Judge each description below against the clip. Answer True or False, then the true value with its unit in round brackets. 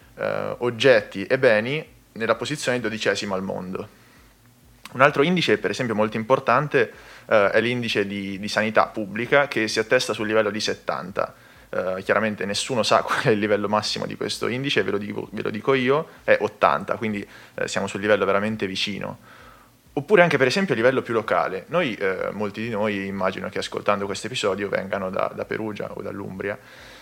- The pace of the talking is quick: True (180 wpm)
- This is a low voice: True (110 Hz)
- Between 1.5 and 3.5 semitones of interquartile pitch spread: False (3.9 semitones)